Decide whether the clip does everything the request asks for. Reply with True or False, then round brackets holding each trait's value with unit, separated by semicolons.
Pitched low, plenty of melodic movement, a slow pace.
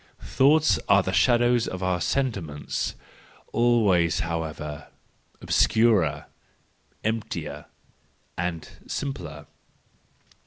True (95 Hz; 6.2 semitones; 80 wpm)